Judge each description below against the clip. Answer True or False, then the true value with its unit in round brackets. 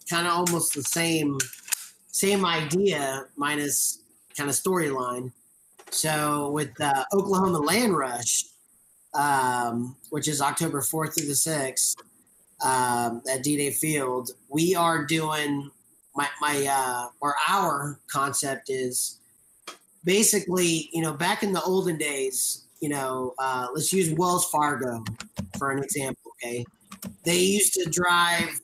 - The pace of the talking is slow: True (130 wpm)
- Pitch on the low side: False (145 Hz)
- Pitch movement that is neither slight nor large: True (4.2 semitones)